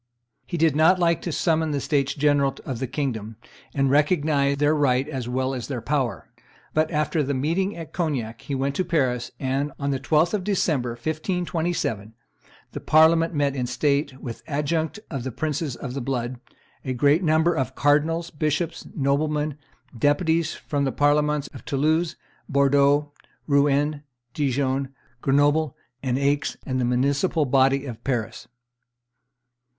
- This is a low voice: No, medium, 145 Hz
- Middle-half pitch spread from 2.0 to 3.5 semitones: Yes, average, 2.9 semitones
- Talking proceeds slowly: No, average, 155 wpm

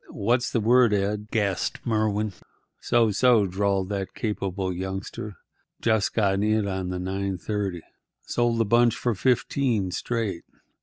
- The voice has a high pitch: No, low, 105 Hz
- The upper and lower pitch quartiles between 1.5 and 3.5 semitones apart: Yes, average, 2.9 semitones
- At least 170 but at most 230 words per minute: No, slow, 135 wpm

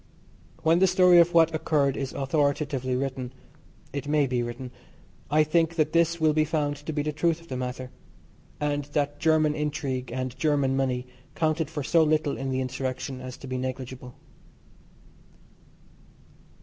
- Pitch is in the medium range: Yes, medium, 145 Hz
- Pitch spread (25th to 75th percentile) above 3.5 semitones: No, average, 3.2 semitones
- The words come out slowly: No, average, 160 wpm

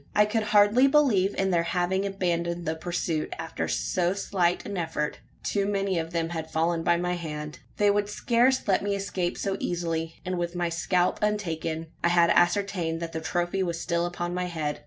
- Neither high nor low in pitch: Yes, medium, 175 Hz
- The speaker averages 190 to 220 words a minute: Yes, average, 195 wpm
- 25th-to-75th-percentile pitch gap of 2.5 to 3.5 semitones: Yes, average, 2.8 semitones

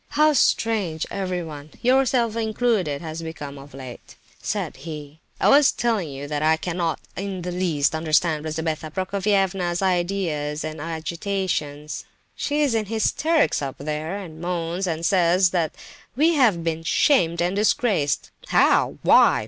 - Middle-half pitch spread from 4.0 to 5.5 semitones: Yes, average, 4.3 semitones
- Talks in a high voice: No, medium, 175 Hz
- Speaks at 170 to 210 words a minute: No, average, 140 wpm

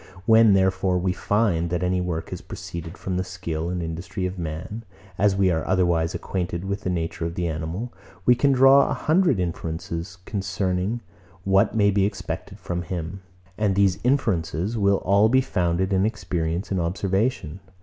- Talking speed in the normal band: Yes, average, 170 wpm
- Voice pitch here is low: Yes, very low, 95 Hz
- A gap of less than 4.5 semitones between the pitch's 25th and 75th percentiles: Yes, average, 2.9 semitones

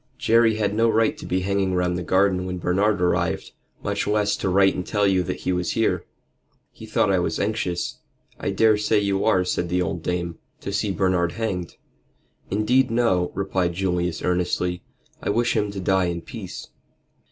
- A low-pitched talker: Yes, very low, 95 Hz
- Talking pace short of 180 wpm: No, average, 185 wpm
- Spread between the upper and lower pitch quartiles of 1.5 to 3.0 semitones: Yes, average, 2.7 semitones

